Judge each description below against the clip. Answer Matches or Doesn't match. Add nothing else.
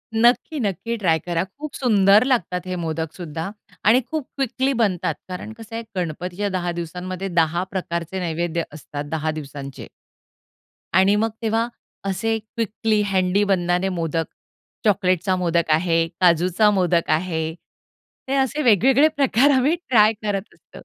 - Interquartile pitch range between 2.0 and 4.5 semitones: Doesn't match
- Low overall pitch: Doesn't match